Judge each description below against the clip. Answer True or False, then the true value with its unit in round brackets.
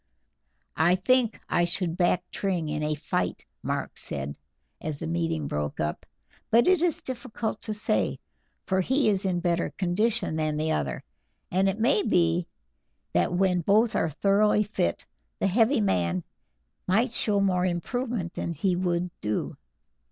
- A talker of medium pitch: True (180 Hz)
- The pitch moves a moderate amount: True (4.6 semitones)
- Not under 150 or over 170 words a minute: True (155 wpm)